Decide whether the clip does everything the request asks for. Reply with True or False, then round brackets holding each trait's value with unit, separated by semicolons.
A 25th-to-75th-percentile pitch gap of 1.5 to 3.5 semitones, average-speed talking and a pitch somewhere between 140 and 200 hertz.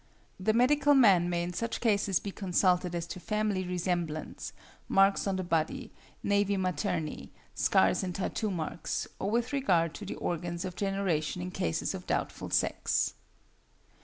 True (2.7 semitones; 155 wpm; 185 Hz)